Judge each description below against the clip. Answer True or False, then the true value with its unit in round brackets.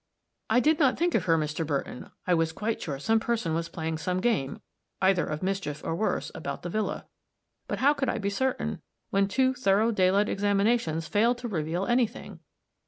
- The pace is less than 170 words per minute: False (195 wpm)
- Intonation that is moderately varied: False (6.2 semitones)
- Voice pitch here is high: True (195 Hz)